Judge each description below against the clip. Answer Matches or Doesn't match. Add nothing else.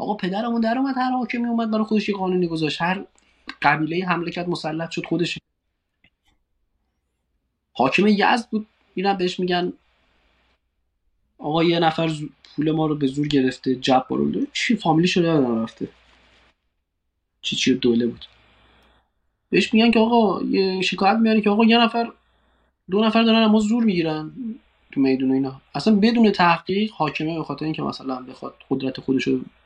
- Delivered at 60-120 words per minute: Doesn't match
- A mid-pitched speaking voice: Matches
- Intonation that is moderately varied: Doesn't match